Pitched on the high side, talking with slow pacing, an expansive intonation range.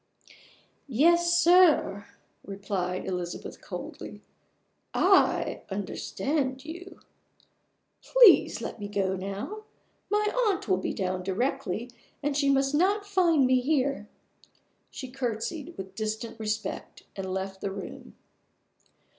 Yes: very high, 255 Hz; slow, 110 wpm; wide, 8.9 semitones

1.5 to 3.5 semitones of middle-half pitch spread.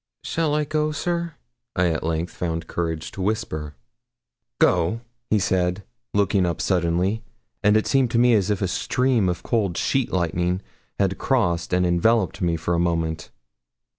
No: average, 4.9 semitones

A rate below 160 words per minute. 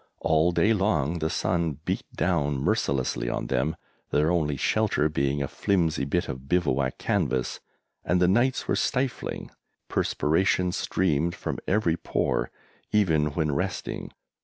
Yes: slow, 135 wpm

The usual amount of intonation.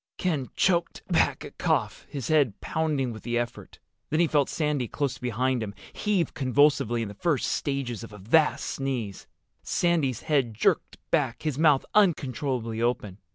Yes: average, 4.2 semitones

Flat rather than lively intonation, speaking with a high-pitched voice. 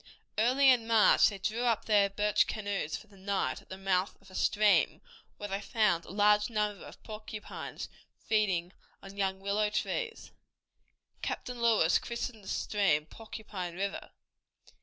Yes: narrow, 2.1 semitones; high, 210 Hz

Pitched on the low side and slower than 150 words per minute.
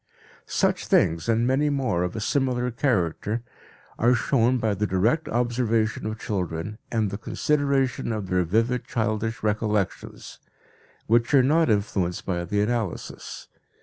Yes: low, 110 Hz; average, 140 wpm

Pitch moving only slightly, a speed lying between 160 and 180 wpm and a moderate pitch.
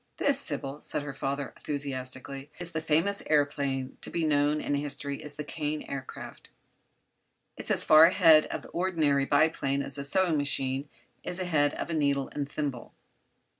Yes: narrow, 2.1 semitones; average, 170 wpm; medium, 145 Hz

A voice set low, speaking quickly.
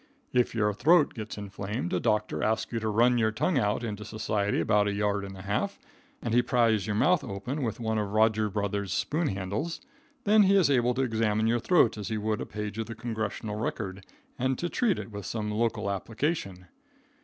Yes: low, 110 Hz; fast, 210 wpm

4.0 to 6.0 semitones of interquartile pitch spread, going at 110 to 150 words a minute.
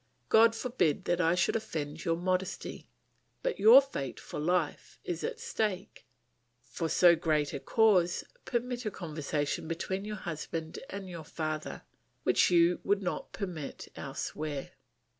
Yes: average, 4.4 semitones; average, 140 wpm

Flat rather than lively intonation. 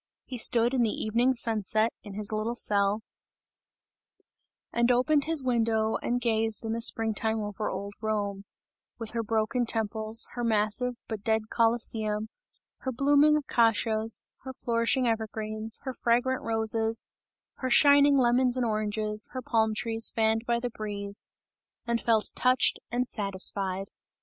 Yes: narrow, 2.1 semitones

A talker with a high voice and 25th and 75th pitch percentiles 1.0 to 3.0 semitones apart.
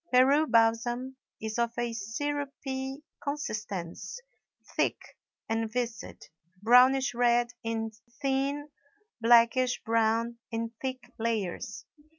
Yes: high, 240 Hz; average, 2.7 semitones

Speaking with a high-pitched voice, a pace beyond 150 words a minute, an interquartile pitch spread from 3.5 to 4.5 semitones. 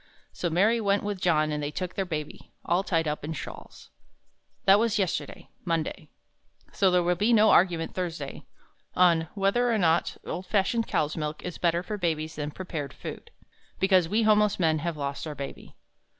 No: medium, 175 Hz; average, 180 wpm; average, 3.9 semitones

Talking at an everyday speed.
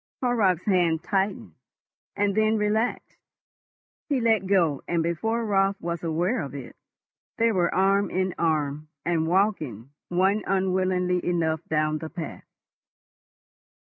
No: slow, 125 wpm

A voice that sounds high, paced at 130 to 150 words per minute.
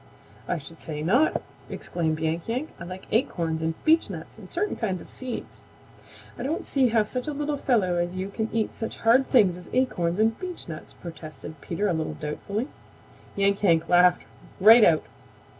No: high, 195 Hz; average, 175 wpm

